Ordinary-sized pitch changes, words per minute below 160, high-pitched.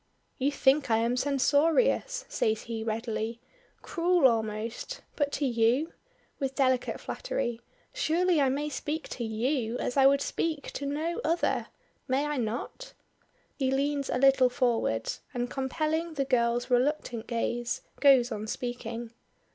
Yes: average, 3.9 semitones; average, 140 wpm; very high, 265 Hz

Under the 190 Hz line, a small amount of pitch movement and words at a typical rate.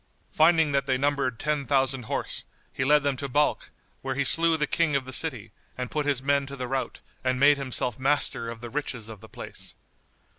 No: medium, 140 Hz; narrow, 2.3 semitones; fast, 215 wpm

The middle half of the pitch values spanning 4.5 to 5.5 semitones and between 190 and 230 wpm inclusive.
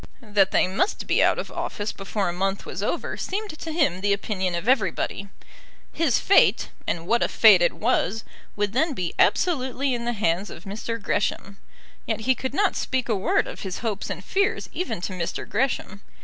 Yes: average, 5.2 semitones; average, 195 wpm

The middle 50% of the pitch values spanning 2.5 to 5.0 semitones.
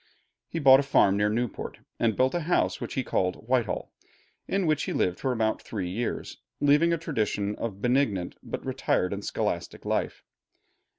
No: wide, 5.6 semitones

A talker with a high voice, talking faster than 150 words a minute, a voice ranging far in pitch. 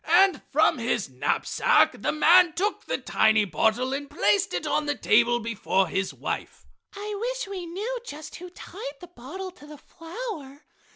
Yes: very high, 300 Hz; average, 170 wpm; wide, 7.7 semitones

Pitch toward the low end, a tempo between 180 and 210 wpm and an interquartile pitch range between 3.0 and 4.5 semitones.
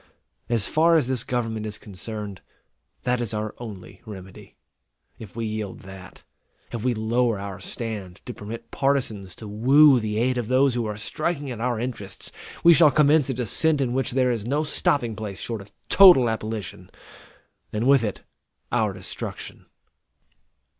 No: low, 115 Hz; average, 165 wpm; average, 3.6 semitones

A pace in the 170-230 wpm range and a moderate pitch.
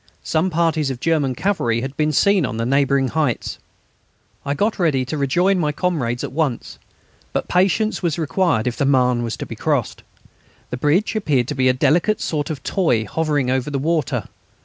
Yes: average, 190 wpm; medium, 145 Hz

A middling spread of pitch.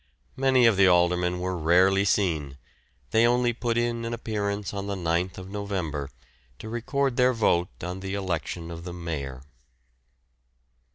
Yes: average, 4.8 semitones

